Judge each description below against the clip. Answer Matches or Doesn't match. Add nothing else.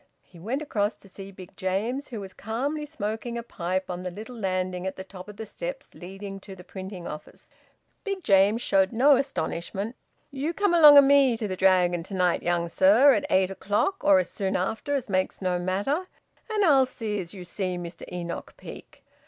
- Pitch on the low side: Doesn't match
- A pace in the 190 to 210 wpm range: Matches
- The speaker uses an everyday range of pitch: Doesn't match